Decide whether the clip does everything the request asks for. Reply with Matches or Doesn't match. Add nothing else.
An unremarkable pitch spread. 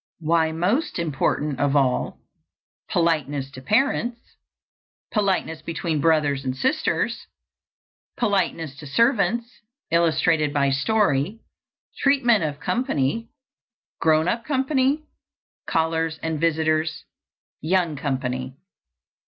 Doesn't match